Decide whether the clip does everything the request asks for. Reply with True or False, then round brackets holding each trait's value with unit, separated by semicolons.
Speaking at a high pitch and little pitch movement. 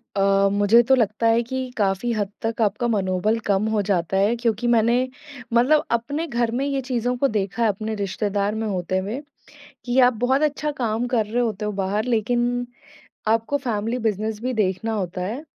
False (225 Hz; 3.0 semitones)